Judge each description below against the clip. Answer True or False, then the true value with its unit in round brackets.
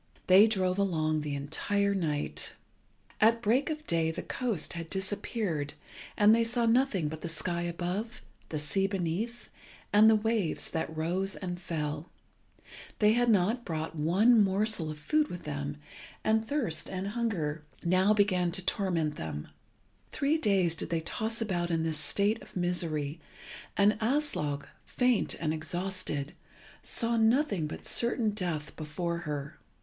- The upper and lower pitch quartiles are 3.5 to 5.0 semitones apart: False (5.5 semitones)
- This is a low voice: False (185 Hz)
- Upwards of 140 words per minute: True (150 wpm)